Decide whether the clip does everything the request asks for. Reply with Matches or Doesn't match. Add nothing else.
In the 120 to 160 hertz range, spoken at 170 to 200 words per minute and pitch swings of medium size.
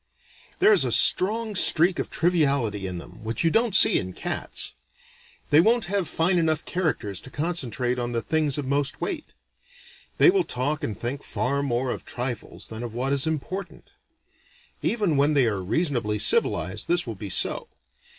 Doesn't match